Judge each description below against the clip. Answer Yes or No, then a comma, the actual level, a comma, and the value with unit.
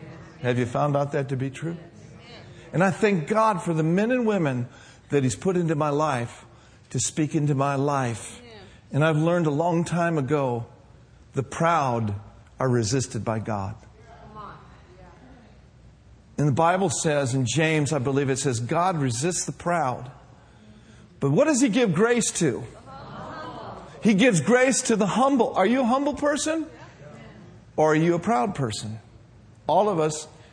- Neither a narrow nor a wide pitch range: No, wide, 6.1 semitones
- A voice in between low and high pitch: Yes, medium, 145 Hz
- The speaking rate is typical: Yes, average, 160 wpm